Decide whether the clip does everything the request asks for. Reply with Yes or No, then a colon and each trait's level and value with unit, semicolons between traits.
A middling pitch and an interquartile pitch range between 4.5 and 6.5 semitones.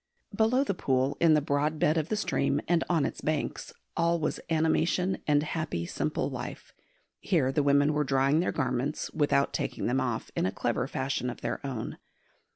No: medium, 145 Hz; average, 3.3 semitones